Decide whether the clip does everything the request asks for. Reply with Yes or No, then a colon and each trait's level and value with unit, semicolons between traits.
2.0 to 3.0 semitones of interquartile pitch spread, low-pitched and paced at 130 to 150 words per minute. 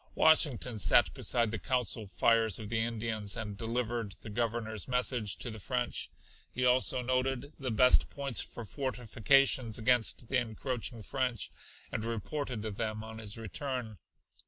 Yes: narrow, 2.6 semitones; low, 115 Hz; average, 145 wpm